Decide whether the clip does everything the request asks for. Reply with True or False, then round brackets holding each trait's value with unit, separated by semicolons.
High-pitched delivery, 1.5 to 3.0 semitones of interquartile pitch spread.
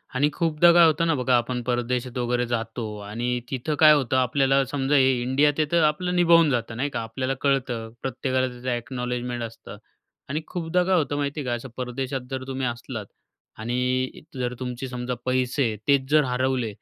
False (130 Hz; 2.7 semitones)